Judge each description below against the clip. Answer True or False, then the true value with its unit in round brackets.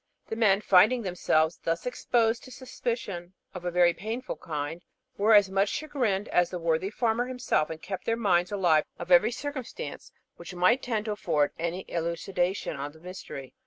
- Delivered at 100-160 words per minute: False (175 wpm)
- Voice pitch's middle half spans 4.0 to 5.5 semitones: True (4.7 semitones)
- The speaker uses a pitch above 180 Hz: True (190 Hz)